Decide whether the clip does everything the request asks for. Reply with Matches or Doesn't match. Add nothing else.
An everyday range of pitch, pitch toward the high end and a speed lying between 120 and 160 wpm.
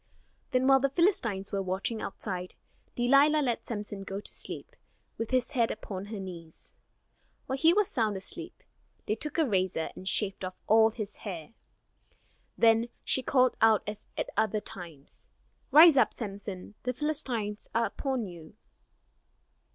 Matches